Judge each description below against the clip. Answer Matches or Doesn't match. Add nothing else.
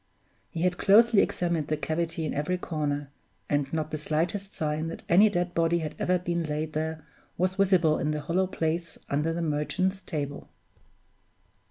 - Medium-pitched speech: Matches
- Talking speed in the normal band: Matches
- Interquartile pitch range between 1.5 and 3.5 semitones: Matches